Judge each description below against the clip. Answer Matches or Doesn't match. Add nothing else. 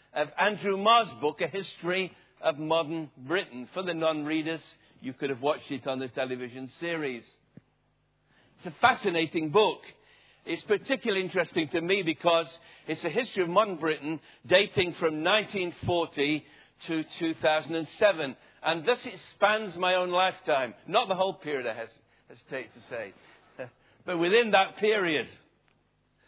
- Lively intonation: Doesn't match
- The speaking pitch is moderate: Matches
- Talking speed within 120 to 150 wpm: Matches